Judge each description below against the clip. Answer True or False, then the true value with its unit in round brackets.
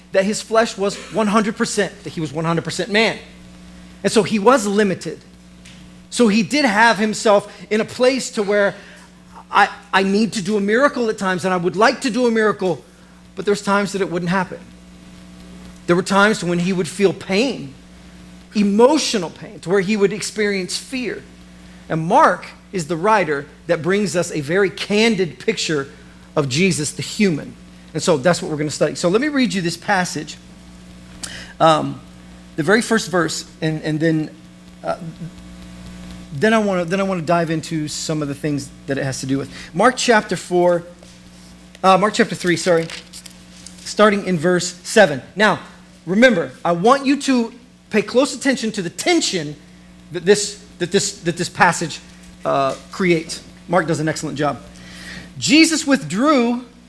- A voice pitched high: False (180 Hz)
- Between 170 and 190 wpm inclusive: True (175 wpm)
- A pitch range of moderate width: False (7.3 semitones)